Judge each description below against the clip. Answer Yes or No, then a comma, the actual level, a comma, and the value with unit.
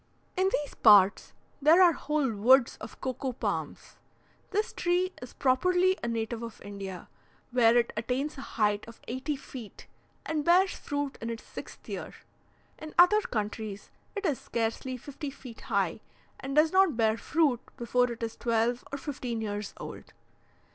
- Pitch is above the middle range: Yes, very high, 250 Hz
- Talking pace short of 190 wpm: Yes, average, 160 wpm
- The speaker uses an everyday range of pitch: Yes, average, 5.0 semitones